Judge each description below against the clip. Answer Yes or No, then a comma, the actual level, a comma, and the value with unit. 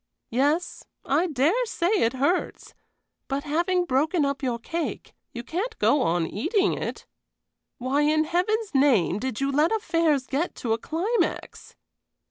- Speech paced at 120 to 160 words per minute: Yes, average, 145 wpm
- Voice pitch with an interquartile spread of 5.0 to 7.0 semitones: Yes, average, 5.3 semitones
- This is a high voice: Yes, very high, 300 Hz